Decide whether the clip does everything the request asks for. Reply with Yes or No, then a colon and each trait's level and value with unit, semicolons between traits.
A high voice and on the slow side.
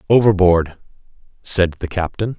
No: very low, 95 Hz; slow, 100 wpm